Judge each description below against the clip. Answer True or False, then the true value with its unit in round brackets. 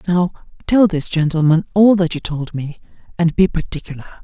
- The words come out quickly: False (170 wpm)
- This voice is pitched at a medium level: True (170 Hz)